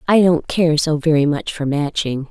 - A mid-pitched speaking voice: Yes, medium, 155 Hz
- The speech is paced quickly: Yes, fast, 210 wpm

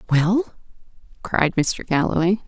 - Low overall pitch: No, medium, 175 Hz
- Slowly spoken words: Yes, slow, 95 wpm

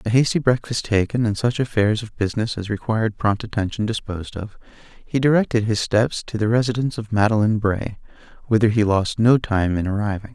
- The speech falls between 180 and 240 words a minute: Yes, average, 185 wpm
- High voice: No, low, 110 Hz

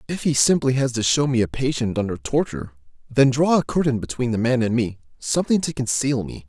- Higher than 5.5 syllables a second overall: Yes, 5.9 syllables/s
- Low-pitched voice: Yes, low, 125 Hz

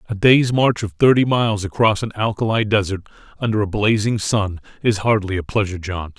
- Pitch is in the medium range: No, low, 105 Hz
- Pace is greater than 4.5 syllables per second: Yes, 5.6 syllables/s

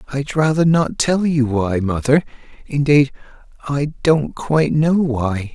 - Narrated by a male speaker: Yes, male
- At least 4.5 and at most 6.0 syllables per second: No, 3.9 syllables/s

